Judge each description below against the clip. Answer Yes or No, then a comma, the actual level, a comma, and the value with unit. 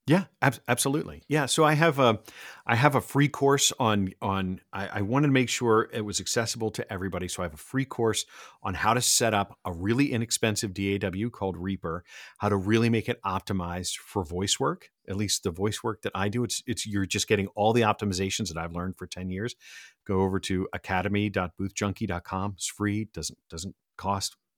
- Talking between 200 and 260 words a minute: Yes, fast, 205 wpm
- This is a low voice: Yes, low, 105 Hz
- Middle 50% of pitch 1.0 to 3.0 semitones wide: No, average, 3.6 semitones